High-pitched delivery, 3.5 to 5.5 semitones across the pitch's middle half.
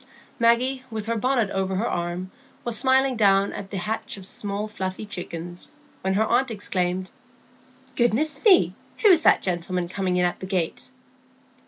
Yes: high, 205 Hz; average, 4.2 semitones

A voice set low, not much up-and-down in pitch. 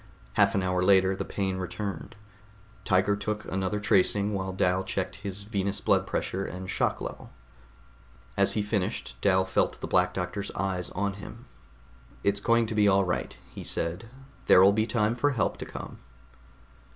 Yes: very low, 95 Hz; narrow, 1.8 semitones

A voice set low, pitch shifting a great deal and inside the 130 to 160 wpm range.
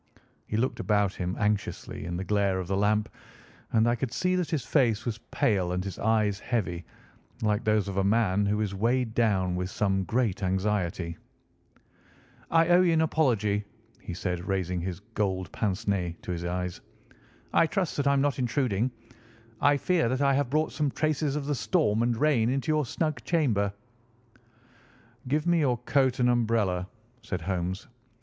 No: low, 110 Hz; wide, 6.1 semitones; average, 180 wpm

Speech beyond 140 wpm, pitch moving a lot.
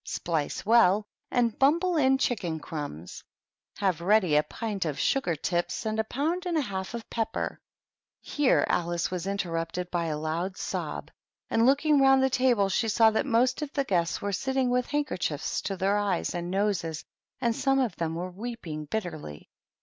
Yes: average, 180 wpm; wide, 6.6 semitones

